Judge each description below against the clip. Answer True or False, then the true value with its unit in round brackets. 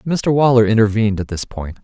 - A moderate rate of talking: True (195 wpm)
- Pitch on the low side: True (110 Hz)